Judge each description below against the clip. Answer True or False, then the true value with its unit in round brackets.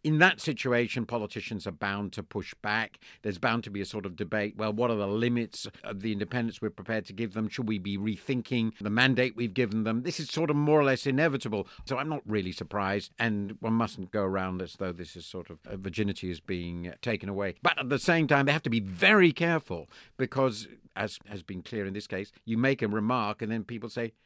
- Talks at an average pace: False (235 wpm)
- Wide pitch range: False (3.8 semitones)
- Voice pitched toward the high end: False (110 Hz)